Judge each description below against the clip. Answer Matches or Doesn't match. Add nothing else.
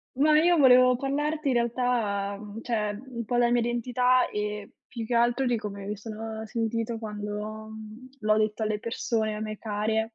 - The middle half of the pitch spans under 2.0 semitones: Doesn't match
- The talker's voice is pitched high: Matches